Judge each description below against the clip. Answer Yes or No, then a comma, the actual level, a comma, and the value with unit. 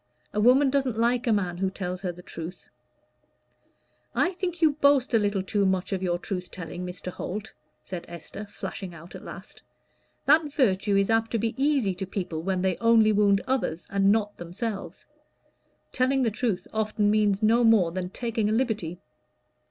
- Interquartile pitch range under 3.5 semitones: No, average, 4.0 semitones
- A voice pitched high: Yes, high, 205 Hz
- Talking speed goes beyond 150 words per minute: Yes, average, 180 wpm